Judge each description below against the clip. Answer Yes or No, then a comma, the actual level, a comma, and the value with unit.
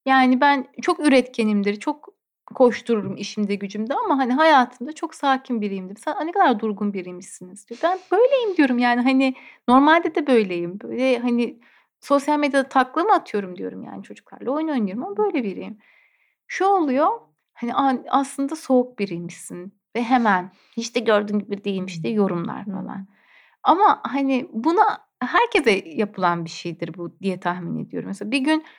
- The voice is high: Yes, very high, 250 Hz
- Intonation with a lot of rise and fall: Yes, wide, 6.6 semitones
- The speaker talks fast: Yes, fast, 150 wpm